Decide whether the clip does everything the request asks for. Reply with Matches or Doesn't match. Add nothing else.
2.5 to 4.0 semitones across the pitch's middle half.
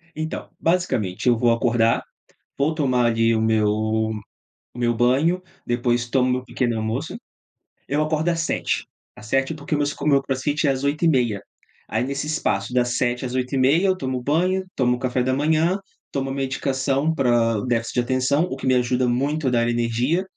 Matches